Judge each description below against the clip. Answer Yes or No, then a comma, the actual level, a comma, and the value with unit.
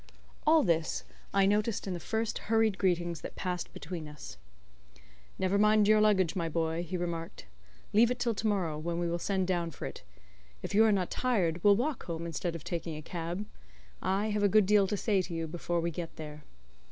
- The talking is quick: Yes, fast, 210 wpm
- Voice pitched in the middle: Yes, medium, 180 Hz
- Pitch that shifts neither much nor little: Yes, average, 3.8 semitones